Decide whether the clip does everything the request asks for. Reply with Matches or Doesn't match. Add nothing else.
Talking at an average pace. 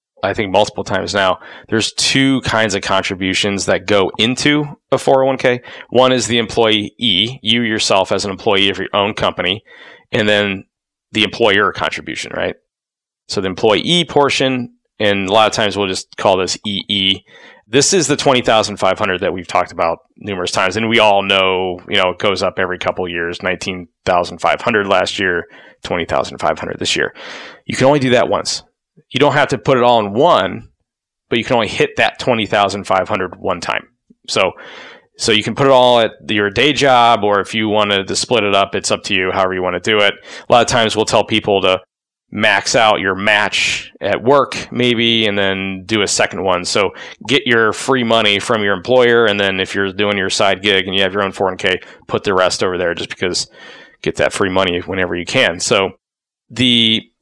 Doesn't match